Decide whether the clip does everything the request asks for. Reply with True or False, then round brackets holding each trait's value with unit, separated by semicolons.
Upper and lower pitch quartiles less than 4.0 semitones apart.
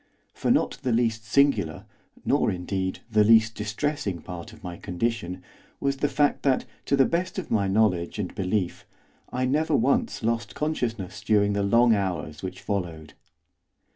False (5.0 semitones)